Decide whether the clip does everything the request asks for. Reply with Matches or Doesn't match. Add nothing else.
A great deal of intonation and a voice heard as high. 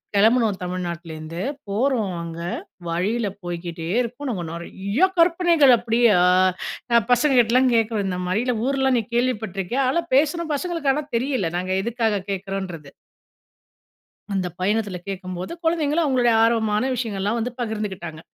Matches